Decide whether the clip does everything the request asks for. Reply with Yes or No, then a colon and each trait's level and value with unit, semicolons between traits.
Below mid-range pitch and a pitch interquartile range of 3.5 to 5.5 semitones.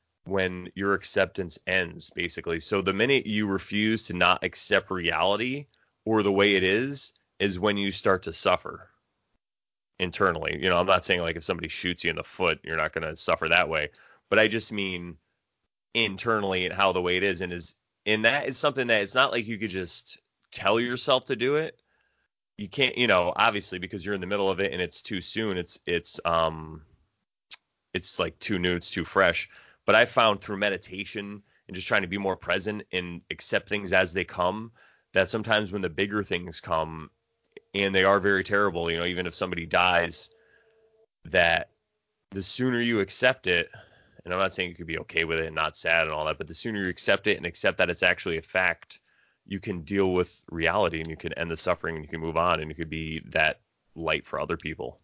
Yes: very low, 95 Hz; average, 3.8 semitones